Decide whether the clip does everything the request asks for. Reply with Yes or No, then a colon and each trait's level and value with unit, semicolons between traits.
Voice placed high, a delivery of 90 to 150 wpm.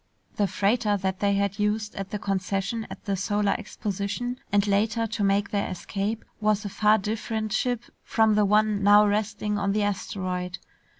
No: high, 205 Hz; average, 175 wpm